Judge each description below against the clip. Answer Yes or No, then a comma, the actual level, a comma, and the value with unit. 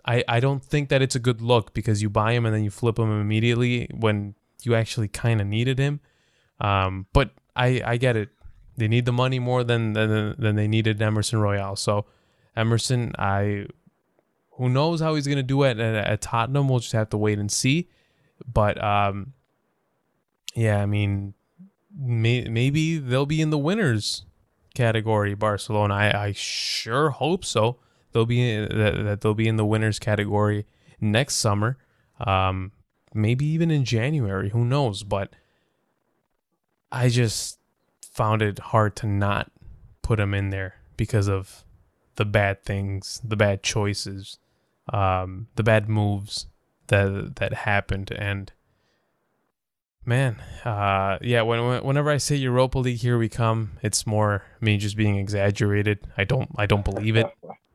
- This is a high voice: No, low, 110 Hz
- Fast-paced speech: No, average, 160 wpm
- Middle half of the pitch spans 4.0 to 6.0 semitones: No, average, 3.2 semitones